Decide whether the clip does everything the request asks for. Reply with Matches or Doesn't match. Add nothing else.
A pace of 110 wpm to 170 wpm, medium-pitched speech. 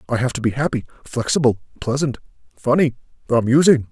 Doesn't match